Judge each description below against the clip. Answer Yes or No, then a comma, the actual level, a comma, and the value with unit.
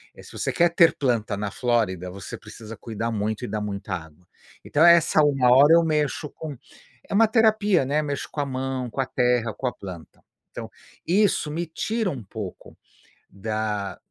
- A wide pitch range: Yes, wide, 6.8 semitones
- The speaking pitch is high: No, low, 125 Hz